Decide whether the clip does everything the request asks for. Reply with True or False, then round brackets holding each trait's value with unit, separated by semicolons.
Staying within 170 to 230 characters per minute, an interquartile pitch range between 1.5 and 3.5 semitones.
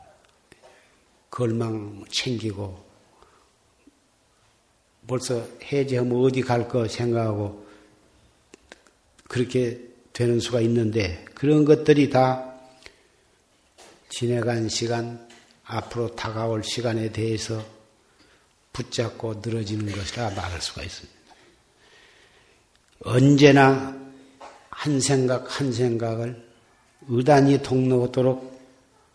True (180 characters per minute; 2.6 semitones)